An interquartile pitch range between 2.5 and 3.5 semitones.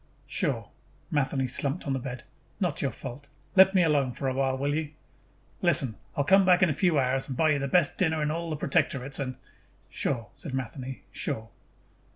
Yes: average, 3.2 semitones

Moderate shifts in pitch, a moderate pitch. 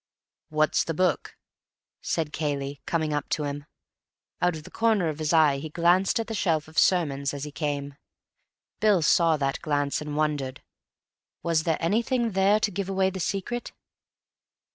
Yes: average, 4.3 semitones; medium, 160 Hz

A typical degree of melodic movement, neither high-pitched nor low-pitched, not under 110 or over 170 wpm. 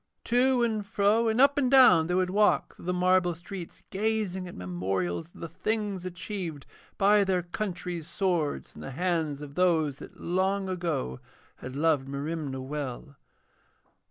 Yes: average, 5.0 semitones; medium, 180 Hz; average, 155 wpm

